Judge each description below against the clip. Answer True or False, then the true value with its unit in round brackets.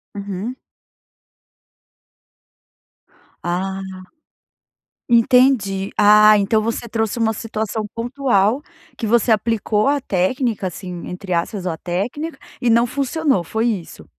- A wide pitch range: False (3.7 semitones)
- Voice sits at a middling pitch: False (220 Hz)